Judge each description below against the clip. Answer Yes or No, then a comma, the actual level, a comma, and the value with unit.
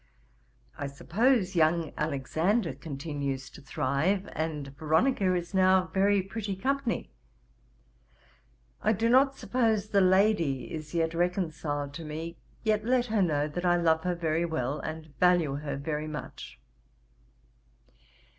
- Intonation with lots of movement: No, average, 4.6 semitones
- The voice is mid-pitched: Yes, medium, 170 Hz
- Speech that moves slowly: Yes, slow, 130 wpm